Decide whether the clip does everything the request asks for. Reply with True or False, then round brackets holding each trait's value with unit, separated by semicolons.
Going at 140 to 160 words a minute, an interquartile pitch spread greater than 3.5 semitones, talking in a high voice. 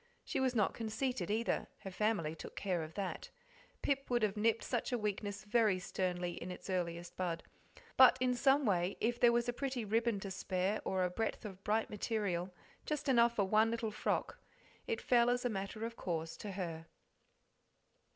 False (190 wpm; 4.3 semitones; 210 Hz)